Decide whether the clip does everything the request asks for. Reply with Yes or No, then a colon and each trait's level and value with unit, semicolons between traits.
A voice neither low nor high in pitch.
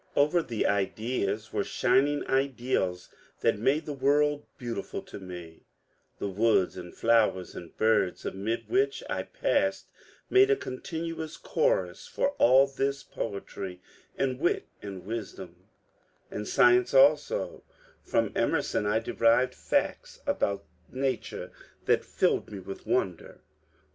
No: low, 120 Hz